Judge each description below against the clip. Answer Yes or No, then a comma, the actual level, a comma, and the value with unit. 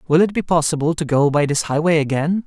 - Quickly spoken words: Yes, fast, 245 wpm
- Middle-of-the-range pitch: Yes, medium, 160 Hz